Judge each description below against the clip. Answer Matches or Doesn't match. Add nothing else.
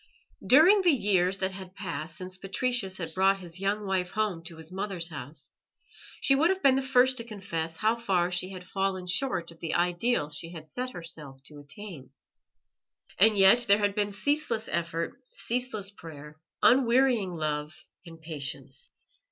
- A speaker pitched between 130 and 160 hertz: Doesn't match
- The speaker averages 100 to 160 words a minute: Doesn't match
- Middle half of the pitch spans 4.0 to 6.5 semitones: Matches